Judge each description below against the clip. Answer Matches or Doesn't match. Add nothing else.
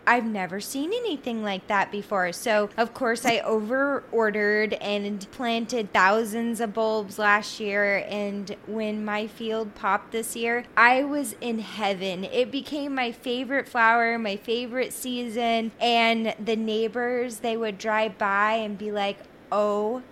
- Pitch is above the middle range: Matches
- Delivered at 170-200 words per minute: Doesn't match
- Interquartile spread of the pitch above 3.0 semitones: Doesn't match